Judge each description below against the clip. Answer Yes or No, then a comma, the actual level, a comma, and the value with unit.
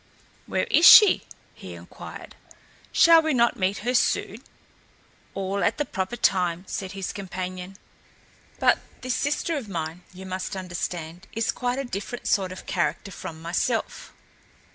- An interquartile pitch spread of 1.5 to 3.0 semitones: No, average, 5.0 semitones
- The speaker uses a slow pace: No, average, 145 wpm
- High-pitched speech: Yes, high, 195 Hz